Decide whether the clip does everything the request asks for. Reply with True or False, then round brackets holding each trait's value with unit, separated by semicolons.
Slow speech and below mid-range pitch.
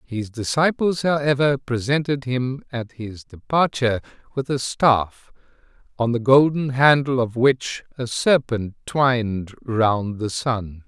True (125 wpm; 125 Hz)